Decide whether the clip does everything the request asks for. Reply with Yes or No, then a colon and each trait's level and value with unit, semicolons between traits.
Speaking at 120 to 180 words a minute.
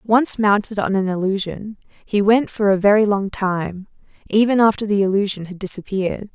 Yes: average, 170 wpm